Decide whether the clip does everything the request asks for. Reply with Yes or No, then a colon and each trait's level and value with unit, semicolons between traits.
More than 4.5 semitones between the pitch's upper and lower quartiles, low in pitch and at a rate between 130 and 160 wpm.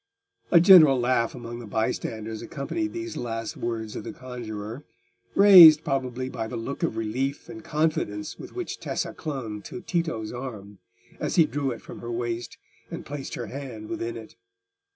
No: average, 5.1 semitones; low, 125 Hz; average, 170 wpm